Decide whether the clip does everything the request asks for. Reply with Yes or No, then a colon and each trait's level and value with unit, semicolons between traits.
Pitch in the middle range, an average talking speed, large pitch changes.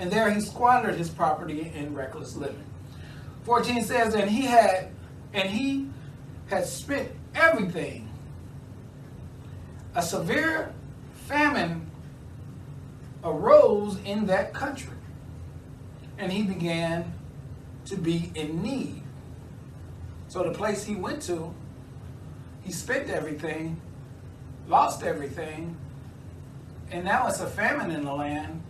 No: medium, 165 Hz; slow, 110 wpm; wide, 7.5 semitones